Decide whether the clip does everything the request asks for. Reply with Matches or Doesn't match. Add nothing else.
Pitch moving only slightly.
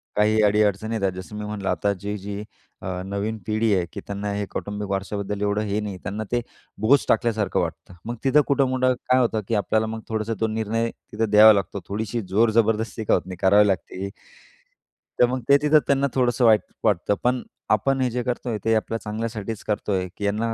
Matches